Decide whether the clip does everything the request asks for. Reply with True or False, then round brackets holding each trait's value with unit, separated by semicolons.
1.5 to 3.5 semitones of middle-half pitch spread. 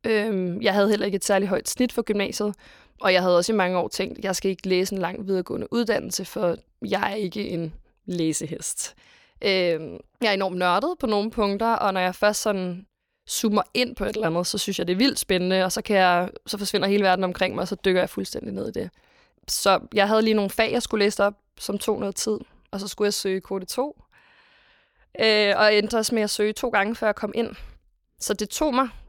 True (2.6 semitones)